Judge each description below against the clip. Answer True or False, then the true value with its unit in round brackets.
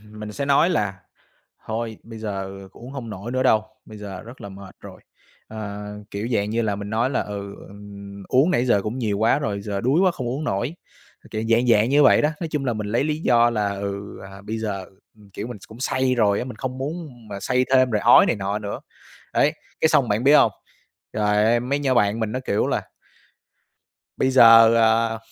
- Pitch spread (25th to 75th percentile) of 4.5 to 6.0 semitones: False (3.8 semitones)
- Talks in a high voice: False (115 Hz)